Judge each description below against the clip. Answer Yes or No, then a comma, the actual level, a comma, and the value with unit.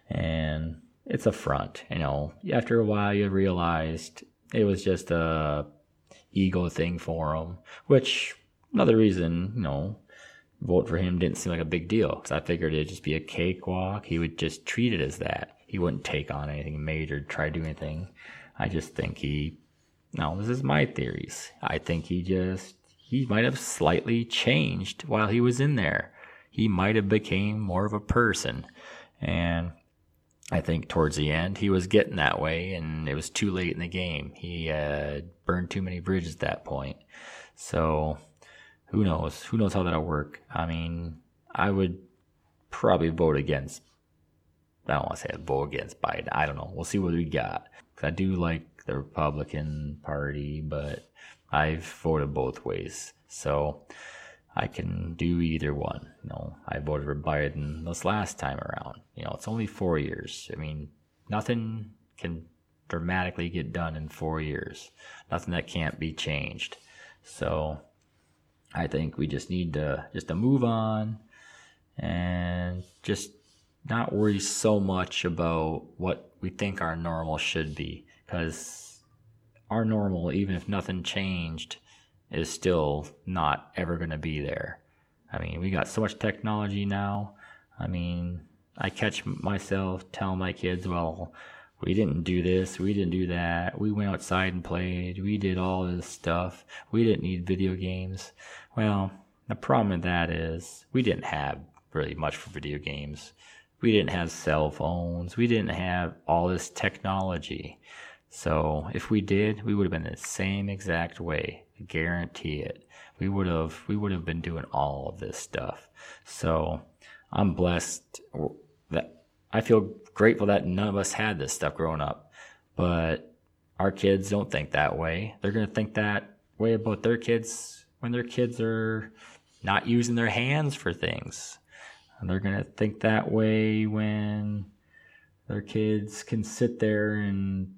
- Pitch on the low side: Yes, very low, 90 Hz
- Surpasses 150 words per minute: Yes, average, 170 wpm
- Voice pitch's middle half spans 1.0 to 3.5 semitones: No, average, 4.3 semitones